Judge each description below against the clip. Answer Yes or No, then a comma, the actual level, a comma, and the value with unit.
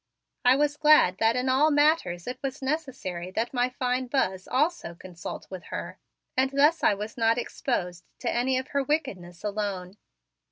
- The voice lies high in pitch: Yes, very high, 250 Hz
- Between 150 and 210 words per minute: Yes, average, 170 wpm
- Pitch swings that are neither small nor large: No, wide, 6.7 semitones